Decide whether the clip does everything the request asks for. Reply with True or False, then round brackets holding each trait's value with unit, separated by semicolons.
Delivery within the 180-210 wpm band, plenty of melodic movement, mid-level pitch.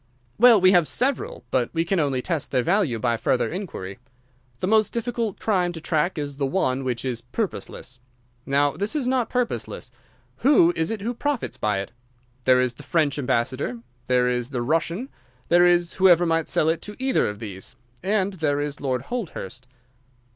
True (185 wpm; 7.6 semitones; 160 Hz)